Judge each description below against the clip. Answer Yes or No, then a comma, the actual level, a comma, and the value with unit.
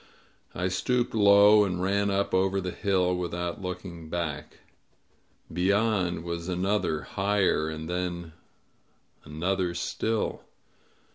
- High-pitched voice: No, very low, 90 Hz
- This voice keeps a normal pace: No, slow, 110 wpm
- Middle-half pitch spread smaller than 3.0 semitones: Yes, narrow, 2.6 semitones